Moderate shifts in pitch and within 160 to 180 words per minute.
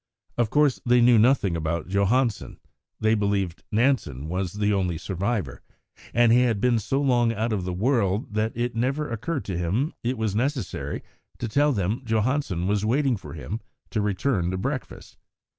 Yes: average, 4.3 semitones; average, 175 wpm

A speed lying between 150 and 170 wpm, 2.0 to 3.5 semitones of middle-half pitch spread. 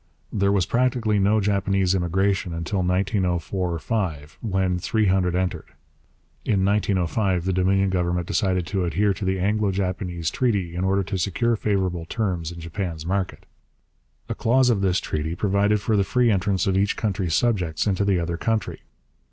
Yes: average, 165 wpm; narrow, 2.4 semitones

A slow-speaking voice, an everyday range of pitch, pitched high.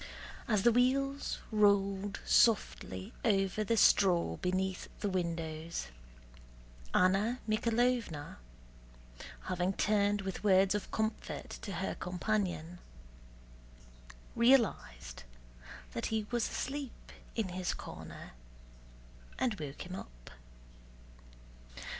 Yes: slow, 95 wpm; average, 3.6 semitones; high, 195 Hz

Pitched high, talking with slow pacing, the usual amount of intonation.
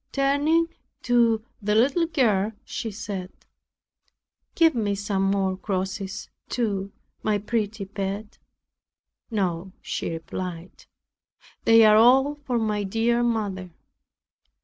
Yes: high, 210 Hz; slow, 100 wpm; average, 3.5 semitones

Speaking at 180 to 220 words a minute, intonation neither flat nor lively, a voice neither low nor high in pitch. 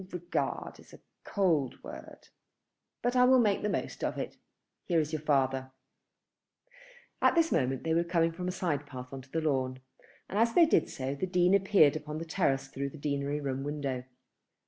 Yes: average, 190 wpm; average, 4.9 semitones; medium, 155 Hz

